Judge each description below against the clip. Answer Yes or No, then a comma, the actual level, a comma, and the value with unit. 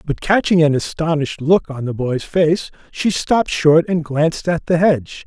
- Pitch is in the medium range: Yes, medium, 160 Hz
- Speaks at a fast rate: No, average, 195 wpm